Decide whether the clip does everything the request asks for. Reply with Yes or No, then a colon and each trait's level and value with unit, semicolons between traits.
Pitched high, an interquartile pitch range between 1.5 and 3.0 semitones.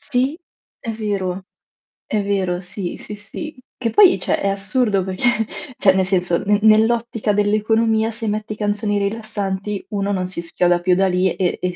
Yes: high, 205 Hz; average, 2.7 semitones